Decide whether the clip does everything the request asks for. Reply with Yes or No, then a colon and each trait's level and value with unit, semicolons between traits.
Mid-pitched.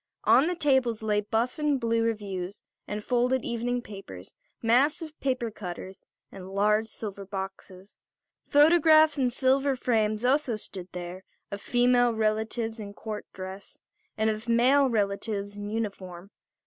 No: high, 220 Hz